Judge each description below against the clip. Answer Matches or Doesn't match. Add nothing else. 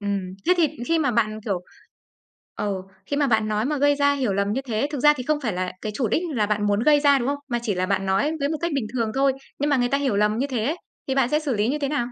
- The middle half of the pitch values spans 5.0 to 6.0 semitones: Matches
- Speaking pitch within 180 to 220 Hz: Doesn't match